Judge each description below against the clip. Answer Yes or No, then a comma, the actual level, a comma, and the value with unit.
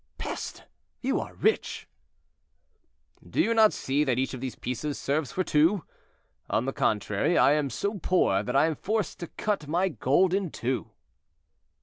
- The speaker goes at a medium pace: Yes, average, 165 wpm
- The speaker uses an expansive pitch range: Yes, wide, 6.3 semitones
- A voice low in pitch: No, medium, 150 Hz